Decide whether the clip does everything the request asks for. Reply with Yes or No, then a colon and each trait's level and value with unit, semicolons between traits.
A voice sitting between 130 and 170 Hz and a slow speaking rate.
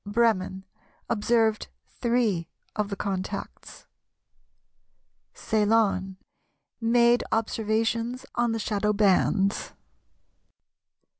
No: high, 220 Hz; slow, 70 wpm